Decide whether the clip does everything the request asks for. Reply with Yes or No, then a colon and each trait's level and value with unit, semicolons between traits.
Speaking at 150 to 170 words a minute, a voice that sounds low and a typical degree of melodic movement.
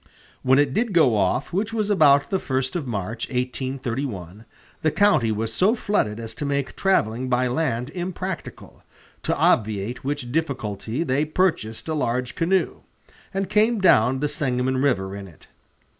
No: average, 160 wpm; low, 130 Hz; wide, 6.2 semitones